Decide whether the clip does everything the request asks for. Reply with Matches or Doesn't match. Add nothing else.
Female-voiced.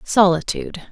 Matches